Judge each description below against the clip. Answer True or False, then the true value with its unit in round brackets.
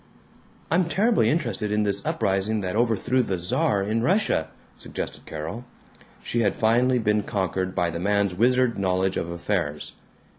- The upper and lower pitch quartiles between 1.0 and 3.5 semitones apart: False (4.2 semitones)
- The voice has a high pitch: False (105 Hz)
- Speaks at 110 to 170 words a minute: True (150 wpm)